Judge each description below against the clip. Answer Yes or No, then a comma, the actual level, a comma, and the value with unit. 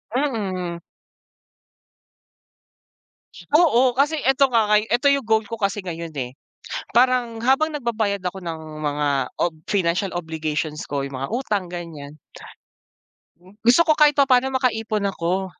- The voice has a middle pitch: No, high, 210 Hz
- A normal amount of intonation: No, wide, 6.8 semitones